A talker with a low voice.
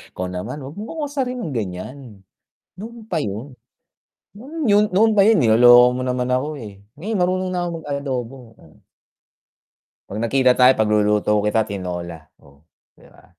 Yes: low, 130 Hz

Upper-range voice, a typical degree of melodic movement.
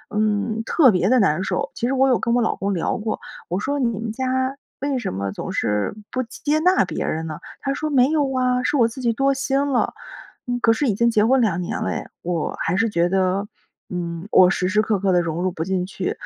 No: high, 220 Hz; wide, 6.0 semitones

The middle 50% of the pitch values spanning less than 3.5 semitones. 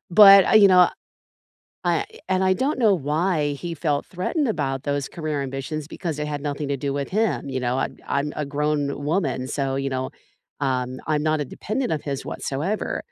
No: average, 4.5 semitones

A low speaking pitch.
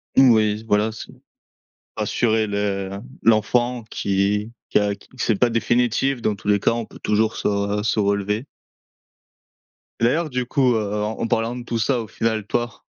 Yes: low, 110 Hz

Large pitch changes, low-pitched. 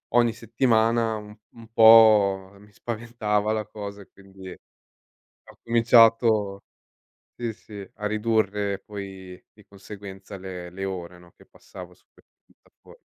No: narrow, 2.5 semitones; low, 105 Hz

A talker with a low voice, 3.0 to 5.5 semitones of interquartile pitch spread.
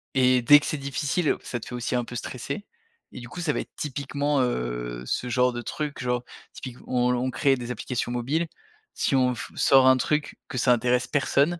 No: low, 125 Hz; narrow, 2.5 semitones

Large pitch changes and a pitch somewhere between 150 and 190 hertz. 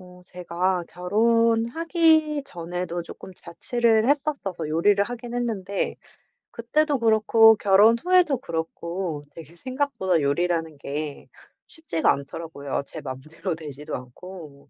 Yes: wide, 6.3 semitones; medium, 185 Hz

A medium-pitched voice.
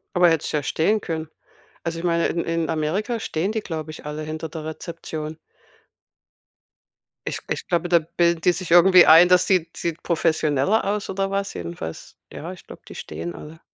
Yes: medium, 165 Hz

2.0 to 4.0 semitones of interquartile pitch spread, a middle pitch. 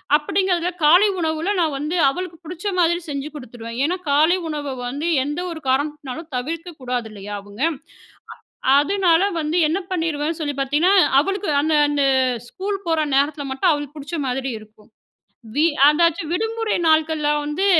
No: average, 3.4 semitones; very high, 310 Hz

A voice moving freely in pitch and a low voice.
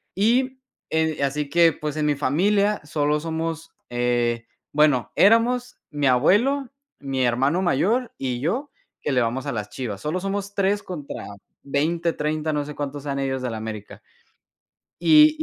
No: wide, 6.6 semitones; medium, 150 Hz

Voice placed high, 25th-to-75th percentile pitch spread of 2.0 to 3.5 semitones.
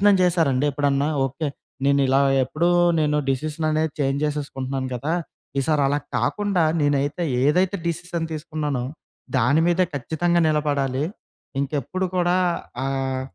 No: medium, 145 Hz; average, 3.1 semitones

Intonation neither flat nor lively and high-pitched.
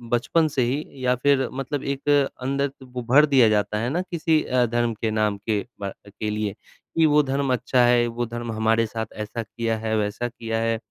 No: average, 3.7 semitones; low, 120 Hz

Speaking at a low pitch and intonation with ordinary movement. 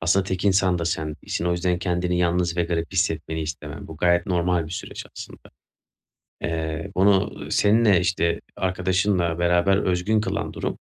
No: very low, 90 Hz; narrow, 1.9 semitones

